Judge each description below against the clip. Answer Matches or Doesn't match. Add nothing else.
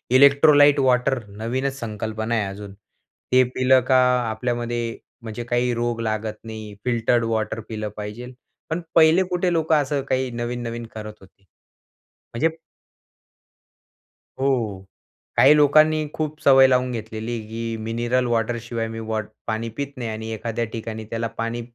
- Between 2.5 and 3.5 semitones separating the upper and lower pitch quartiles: Matches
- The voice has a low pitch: Matches